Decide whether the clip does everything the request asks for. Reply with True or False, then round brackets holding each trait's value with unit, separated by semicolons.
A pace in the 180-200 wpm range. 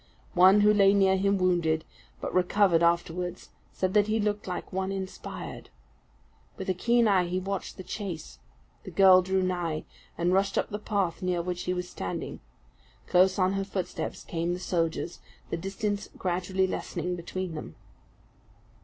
False (160 wpm)